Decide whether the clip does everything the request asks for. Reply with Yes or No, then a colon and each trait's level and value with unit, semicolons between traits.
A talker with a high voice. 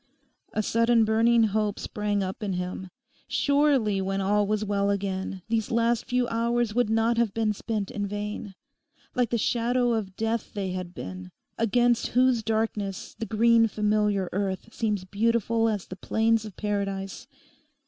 Yes: high, 215 Hz